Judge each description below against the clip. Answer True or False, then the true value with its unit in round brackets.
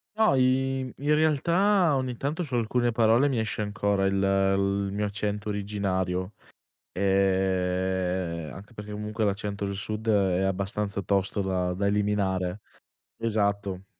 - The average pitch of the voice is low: True (100 Hz)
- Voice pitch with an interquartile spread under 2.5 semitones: False (2.8 semitones)